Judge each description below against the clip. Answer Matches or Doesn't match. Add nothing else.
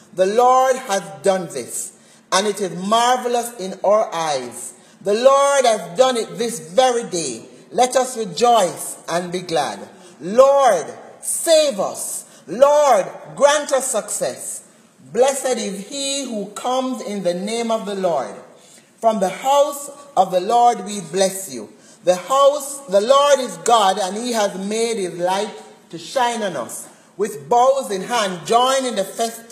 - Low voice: Doesn't match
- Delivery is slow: Doesn't match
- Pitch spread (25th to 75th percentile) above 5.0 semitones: Matches